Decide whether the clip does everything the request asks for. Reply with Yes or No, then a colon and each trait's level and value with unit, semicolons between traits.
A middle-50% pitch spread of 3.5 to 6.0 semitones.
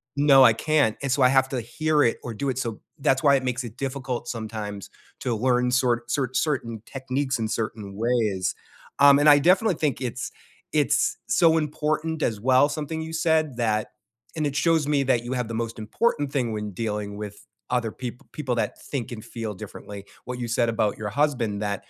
Yes: average, 4.2 semitones